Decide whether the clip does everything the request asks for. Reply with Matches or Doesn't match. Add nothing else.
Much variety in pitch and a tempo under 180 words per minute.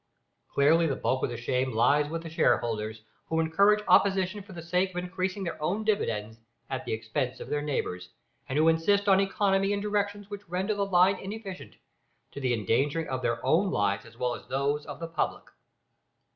Doesn't match